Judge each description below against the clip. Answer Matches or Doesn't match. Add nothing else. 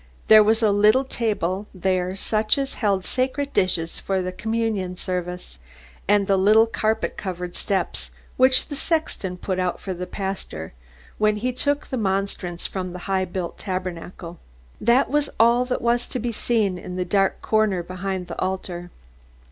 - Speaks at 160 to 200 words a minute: Matches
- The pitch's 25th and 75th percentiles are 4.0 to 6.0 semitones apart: Doesn't match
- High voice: Matches